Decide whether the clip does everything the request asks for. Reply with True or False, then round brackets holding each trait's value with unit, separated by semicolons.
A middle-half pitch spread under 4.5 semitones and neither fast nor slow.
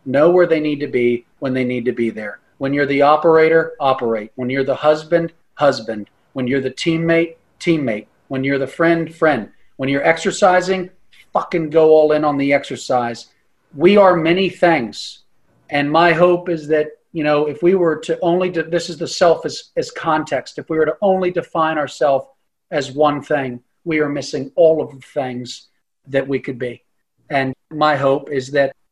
True (3.6 semitones; 190 wpm)